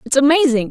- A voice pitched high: Yes, very high, 255 Hz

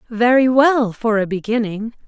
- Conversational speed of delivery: Yes, average, 145 wpm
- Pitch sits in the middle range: No, high, 230 Hz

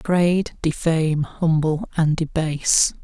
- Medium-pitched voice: Yes, medium, 160 Hz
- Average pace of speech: No, slow, 100 wpm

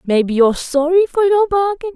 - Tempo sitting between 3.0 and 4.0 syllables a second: No, 5.4 syllables/s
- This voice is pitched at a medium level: No, very high, 335 Hz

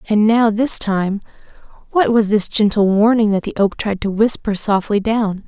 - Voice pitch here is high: Yes, high, 215 Hz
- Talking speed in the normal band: Yes, average, 185 wpm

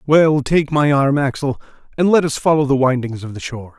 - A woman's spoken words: No, male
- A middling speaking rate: No, fast, 220 wpm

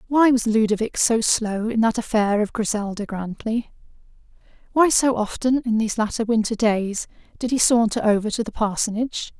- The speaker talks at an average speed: Yes, average, 165 wpm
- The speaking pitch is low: No, high, 225 Hz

